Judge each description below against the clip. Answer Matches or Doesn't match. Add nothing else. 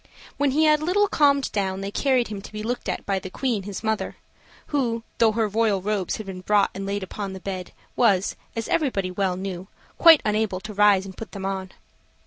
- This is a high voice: Matches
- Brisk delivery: Matches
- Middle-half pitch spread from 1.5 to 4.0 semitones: Matches